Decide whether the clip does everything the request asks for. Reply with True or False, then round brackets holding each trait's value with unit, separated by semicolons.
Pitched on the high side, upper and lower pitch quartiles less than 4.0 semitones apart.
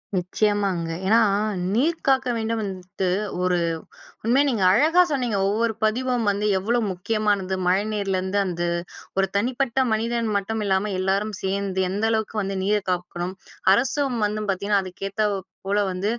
True (205 Hz; 3.2 semitones)